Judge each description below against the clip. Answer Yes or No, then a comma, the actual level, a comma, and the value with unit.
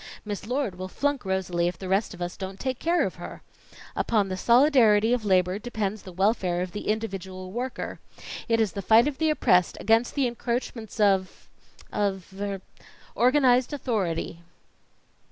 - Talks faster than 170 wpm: No, average, 165 wpm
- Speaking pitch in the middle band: No, high, 210 Hz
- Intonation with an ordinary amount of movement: Yes, average, 4.5 semitones